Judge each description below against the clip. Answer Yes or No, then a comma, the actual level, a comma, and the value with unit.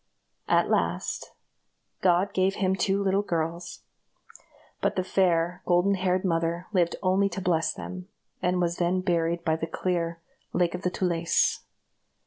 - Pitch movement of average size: No, narrow, 1.7 semitones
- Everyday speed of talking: Yes, average, 145 wpm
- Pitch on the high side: No, medium, 180 Hz